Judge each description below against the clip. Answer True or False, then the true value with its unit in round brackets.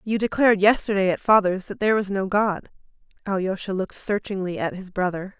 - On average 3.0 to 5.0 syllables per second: False (5.9 syllables/s)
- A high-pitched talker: True (195 Hz)